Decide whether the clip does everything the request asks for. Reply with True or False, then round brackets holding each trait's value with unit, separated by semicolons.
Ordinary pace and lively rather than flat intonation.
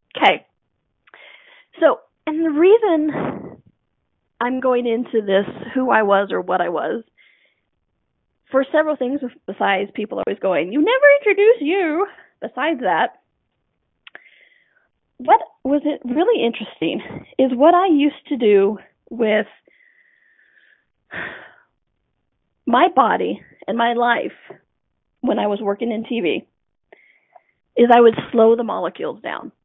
False (120 wpm; 7.6 semitones)